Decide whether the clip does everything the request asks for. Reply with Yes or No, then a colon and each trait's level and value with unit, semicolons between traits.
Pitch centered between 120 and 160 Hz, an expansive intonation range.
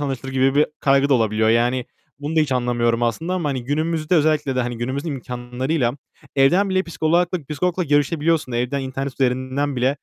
No: low, 135 Hz; average, 3.8 semitones